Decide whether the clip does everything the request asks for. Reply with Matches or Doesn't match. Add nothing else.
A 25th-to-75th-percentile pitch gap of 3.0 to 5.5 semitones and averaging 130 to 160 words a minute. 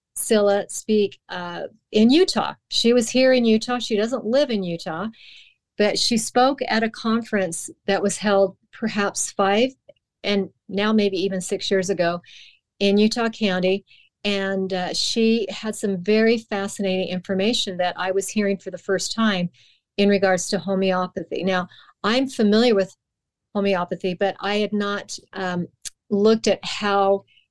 Doesn't match